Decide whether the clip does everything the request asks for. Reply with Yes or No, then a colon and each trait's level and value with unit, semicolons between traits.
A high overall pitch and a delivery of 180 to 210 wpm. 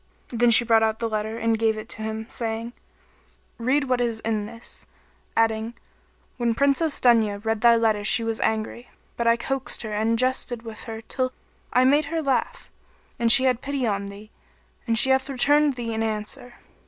Yes: high, 230 Hz; average, 190 wpm